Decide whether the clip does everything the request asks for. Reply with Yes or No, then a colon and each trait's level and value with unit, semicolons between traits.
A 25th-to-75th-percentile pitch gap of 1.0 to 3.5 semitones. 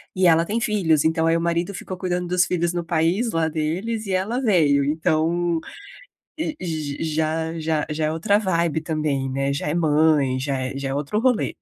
Yes: average, 2.7 semitones